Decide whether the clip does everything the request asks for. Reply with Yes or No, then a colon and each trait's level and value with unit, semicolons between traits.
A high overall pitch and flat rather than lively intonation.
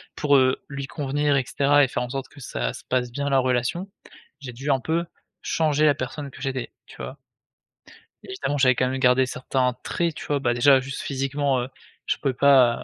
No: low, 135 Hz; narrow, 2.0 semitones